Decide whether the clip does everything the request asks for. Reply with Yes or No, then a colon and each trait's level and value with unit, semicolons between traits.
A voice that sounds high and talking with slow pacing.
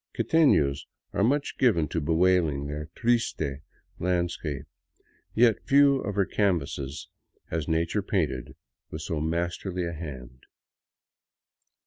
No: very low, 85 Hz; slow, 125 wpm